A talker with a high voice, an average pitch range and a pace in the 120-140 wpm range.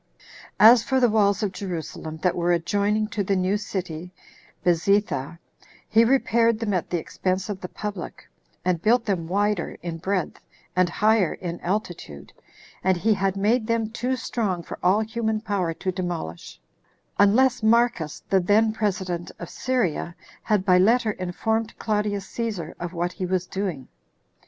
No: high, 200 Hz; average, 3.7 semitones; average, 160 wpm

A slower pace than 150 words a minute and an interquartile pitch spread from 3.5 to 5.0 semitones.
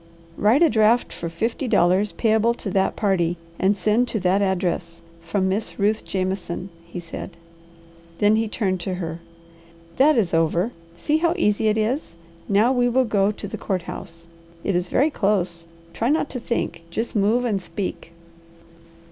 No: average, 170 wpm; average, 4.1 semitones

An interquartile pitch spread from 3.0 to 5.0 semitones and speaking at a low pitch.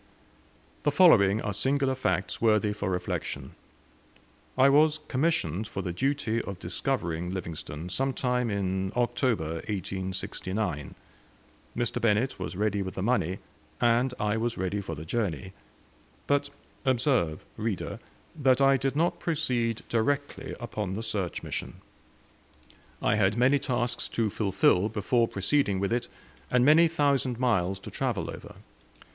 No: wide, 5.5 semitones; low, 110 Hz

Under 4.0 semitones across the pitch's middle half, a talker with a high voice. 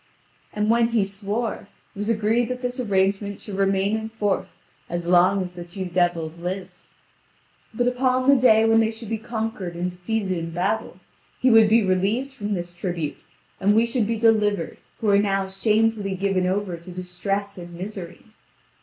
Yes: average, 3.5 semitones; high, 200 Hz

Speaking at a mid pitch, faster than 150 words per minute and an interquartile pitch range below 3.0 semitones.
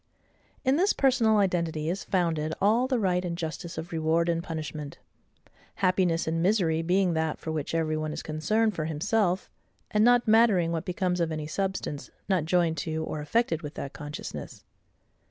No: medium, 170 Hz; average, 170 wpm; average, 3.7 semitones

